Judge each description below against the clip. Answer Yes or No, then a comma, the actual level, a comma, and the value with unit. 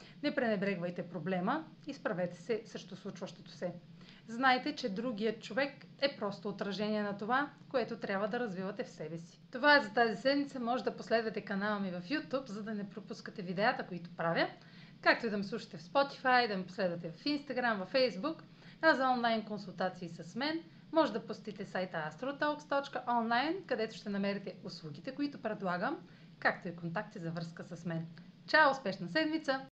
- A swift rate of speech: Yes, fast, 170 wpm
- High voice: Yes, high, 215 Hz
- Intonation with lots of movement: Yes, wide, 5.7 semitones